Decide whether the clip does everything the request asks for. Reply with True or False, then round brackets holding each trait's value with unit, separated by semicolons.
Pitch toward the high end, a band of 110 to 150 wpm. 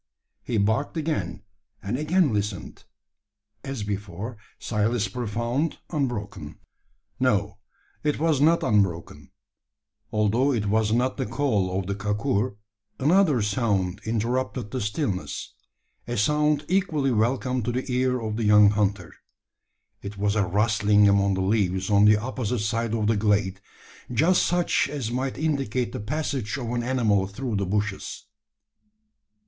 False (110 Hz; 140 wpm)